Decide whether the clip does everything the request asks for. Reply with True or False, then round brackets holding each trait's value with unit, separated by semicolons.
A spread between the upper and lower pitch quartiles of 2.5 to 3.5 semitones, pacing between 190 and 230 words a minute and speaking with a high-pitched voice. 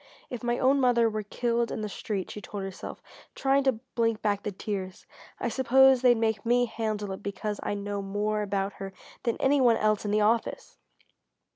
True (2.8 semitones; 195 wpm; 215 Hz)